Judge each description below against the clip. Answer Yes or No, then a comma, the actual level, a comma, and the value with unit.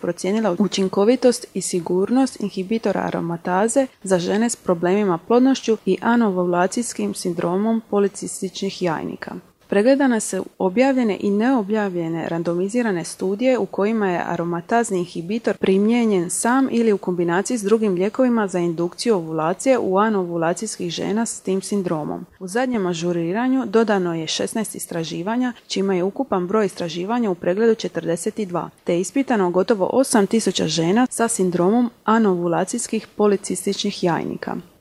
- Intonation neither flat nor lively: Yes, average, 4.0 semitones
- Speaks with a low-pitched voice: No, high, 200 Hz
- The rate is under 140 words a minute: Yes, average, 120 wpm